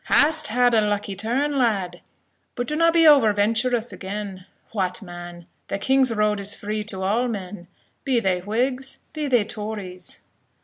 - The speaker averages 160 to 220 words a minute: Yes, average, 165 wpm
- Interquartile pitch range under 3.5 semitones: No, average, 4.3 semitones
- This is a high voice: Yes, high, 215 Hz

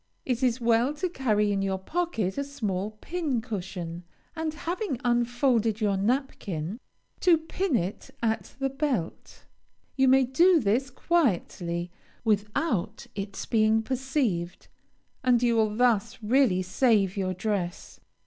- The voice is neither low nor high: No, high, 230 Hz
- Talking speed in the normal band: No, slow, 130 wpm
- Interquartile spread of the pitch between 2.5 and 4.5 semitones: No, average, 5.3 semitones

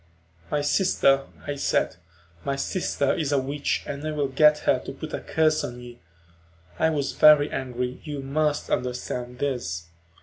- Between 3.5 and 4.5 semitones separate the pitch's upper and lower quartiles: No, average, 3.0 semitones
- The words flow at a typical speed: Yes, average, 165 wpm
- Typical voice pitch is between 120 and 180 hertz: Yes, medium, 140 Hz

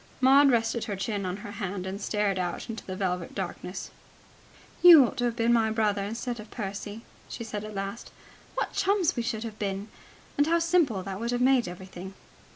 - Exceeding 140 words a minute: Yes, average, 200 wpm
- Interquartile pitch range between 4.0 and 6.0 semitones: No, average, 3.5 semitones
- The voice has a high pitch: Yes, high, 215 Hz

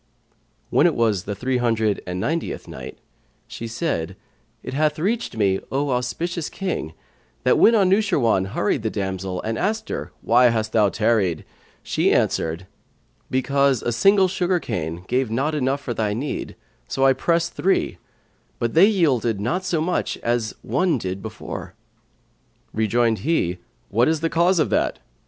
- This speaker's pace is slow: No, average, 155 wpm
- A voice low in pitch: Yes, low, 125 Hz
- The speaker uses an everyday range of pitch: No, wide, 7.3 semitones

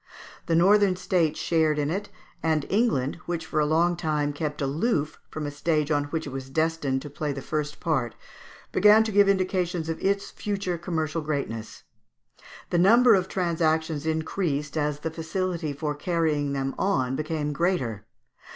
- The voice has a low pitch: No, medium, 160 Hz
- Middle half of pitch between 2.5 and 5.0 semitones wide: Yes, average, 3.4 semitones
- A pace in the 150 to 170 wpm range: Yes, average, 165 wpm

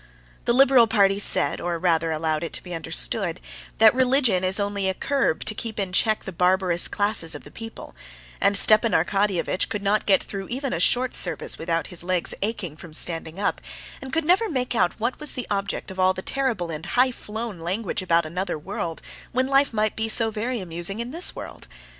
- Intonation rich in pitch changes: No, average, 5.0 semitones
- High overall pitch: Yes, high, 200 Hz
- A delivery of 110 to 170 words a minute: No, fast, 205 wpm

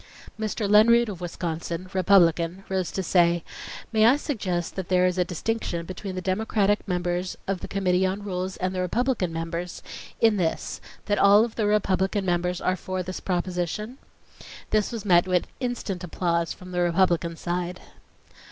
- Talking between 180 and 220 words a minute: No, average, 165 wpm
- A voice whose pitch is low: No, medium, 185 Hz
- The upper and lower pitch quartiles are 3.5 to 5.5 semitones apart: No, average, 2.7 semitones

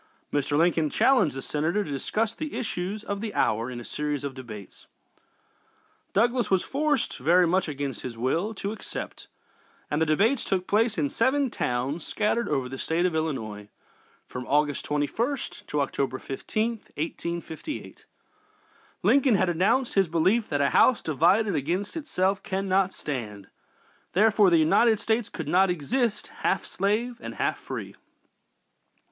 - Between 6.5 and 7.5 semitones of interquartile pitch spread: Yes, wide, 7.1 semitones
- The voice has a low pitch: No, medium, 180 Hz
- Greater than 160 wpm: No, average, 150 wpm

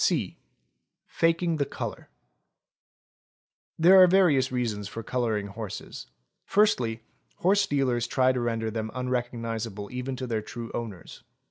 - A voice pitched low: Yes, low, 120 Hz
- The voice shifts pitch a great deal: No, average, 3.8 semitones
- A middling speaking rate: No, slow, 130 wpm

